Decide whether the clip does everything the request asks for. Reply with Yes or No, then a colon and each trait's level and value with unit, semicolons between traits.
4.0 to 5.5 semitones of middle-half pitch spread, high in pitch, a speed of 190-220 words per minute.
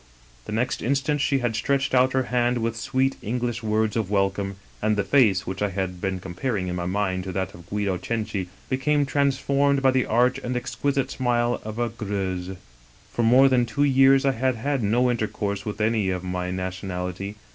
No: average, 5.2 semitones; low, 110 Hz; average, 200 wpm